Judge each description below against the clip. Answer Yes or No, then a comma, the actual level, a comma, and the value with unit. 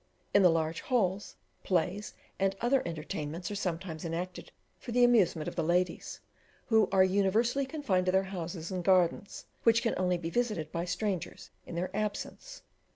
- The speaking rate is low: No, average, 165 wpm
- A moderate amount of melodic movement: Yes, average, 3.8 semitones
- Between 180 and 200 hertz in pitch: Yes, medium, 185 Hz